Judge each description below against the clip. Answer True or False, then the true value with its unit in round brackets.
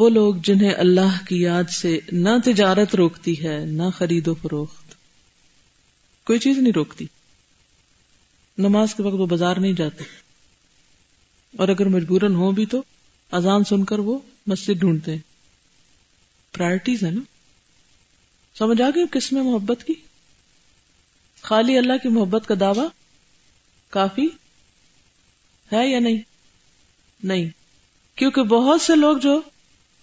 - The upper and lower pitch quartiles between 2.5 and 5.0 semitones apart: False (5.4 semitones)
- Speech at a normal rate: True (130 wpm)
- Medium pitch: False (200 Hz)